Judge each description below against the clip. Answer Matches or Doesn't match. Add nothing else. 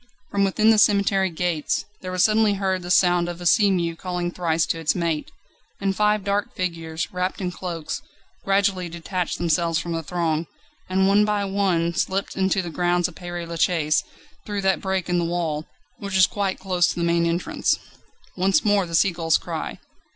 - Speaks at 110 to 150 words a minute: Doesn't match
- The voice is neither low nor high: Matches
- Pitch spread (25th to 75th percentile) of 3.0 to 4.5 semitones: Doesn't match